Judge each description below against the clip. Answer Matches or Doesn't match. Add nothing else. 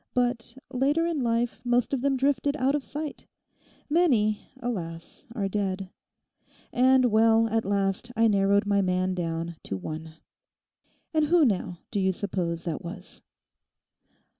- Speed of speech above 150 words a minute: Doesn't match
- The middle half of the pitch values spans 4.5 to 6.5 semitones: Matches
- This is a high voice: Matches